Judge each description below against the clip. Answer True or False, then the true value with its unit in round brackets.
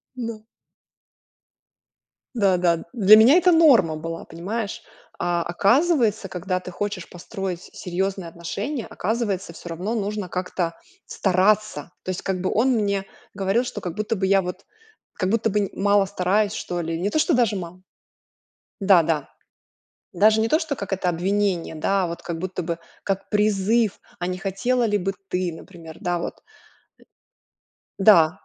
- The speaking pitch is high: True (195 Hz)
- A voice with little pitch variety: False (3.3 semitones)